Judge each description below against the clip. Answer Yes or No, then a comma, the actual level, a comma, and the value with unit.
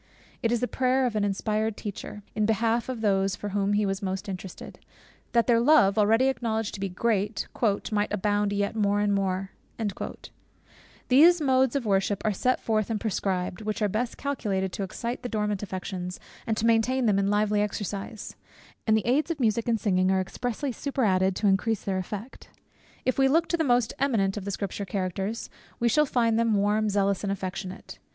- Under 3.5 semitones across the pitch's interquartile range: Yes, average, 3.1 semitones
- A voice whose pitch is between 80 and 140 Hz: No, high, 210 Hz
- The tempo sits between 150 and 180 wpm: No, average, 190 wpm